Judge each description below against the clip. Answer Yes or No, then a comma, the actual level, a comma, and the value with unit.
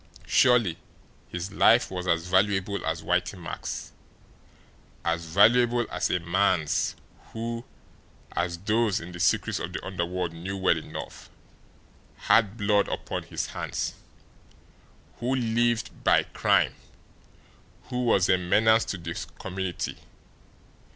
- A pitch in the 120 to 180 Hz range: No, very low, 95 Hz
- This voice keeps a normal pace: No, slow, 120 wpm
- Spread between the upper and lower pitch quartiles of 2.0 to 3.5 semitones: No, average, 4.3 semitones